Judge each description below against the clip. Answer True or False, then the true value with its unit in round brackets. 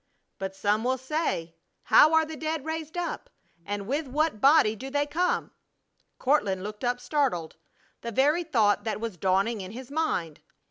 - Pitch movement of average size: False (7.0 semitones)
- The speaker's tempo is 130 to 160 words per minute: False (170 wpm)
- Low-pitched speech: False (255 Hz)